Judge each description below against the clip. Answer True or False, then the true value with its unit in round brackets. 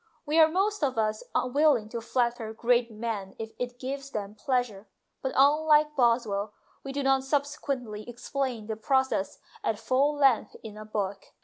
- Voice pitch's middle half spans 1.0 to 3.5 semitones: False (4.2 semitones)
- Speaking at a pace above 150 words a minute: True (165 wpm)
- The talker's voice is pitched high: True (245 Hz)